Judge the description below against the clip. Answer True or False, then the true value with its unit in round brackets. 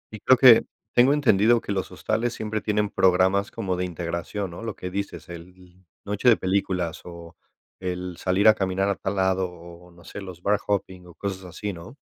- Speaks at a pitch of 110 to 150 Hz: False (95 Hz)